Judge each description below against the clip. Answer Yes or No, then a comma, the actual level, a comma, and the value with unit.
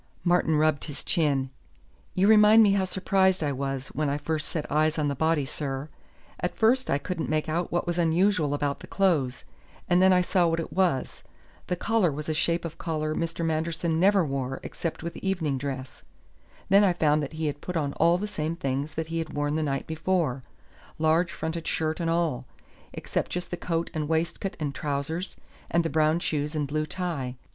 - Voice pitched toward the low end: No, medium, 160 Hz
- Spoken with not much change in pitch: No, average, 3.1 semitones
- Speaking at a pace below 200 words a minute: No, fast, 205 wpm